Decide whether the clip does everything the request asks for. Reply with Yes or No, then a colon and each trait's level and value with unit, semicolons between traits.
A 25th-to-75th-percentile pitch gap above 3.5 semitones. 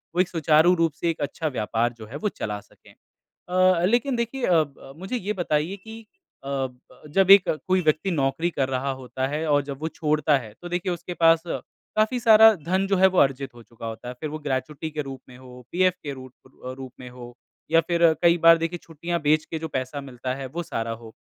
Yes: average, 5.2 semitones